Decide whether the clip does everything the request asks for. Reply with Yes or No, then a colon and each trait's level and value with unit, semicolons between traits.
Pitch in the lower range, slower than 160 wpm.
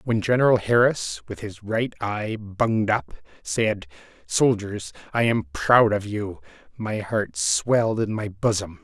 Yes: low, 110 Hz; average, 150 wpm